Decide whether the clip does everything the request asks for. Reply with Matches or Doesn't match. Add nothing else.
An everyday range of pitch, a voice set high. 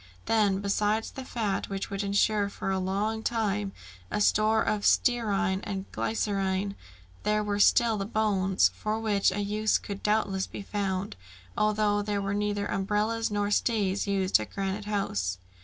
Doesn't match